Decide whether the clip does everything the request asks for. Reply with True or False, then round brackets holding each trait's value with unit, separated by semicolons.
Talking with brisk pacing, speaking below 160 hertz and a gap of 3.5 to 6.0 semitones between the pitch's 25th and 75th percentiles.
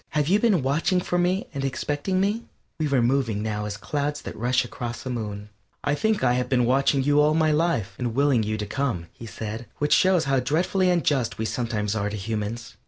True (225 wpm; 135 Hz; 5.5 semitones)